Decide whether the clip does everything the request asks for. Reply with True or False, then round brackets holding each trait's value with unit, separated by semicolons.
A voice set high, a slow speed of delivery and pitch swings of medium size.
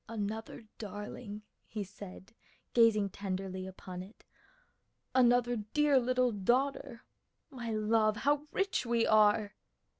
True (220 Hz; 110 wpm; 3.2 semitones)